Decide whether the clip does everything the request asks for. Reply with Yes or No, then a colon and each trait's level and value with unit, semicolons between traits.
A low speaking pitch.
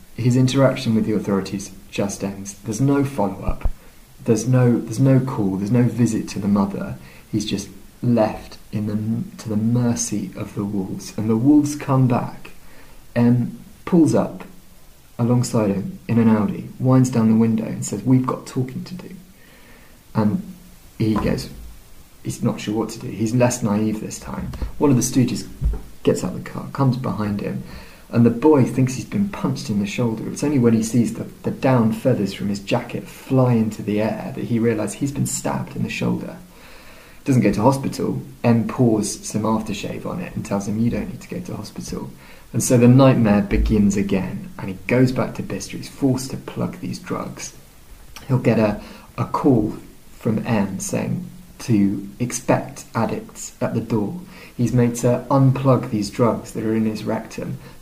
Yes: low, 115 Hz